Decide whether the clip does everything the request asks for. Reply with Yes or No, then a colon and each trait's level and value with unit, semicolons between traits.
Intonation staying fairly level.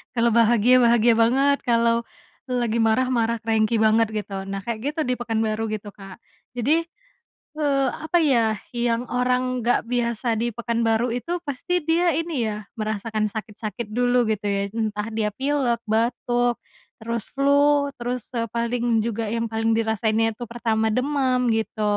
Yes: narrow, 2.1 semitones